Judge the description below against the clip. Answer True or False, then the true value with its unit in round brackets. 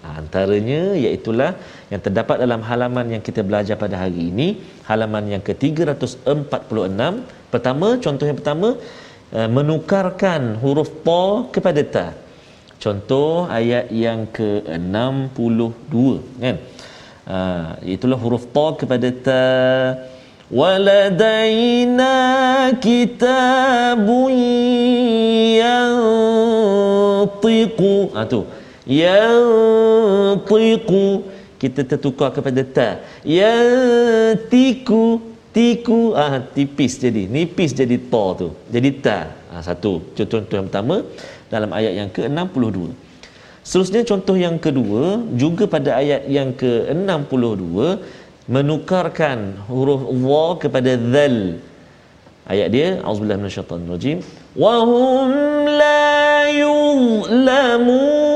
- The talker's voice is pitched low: False (150 Hz)